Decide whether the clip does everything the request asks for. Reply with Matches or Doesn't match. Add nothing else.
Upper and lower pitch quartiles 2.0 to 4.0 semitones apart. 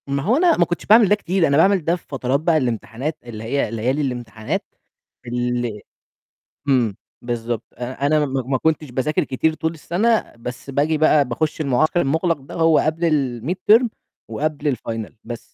Doesn't match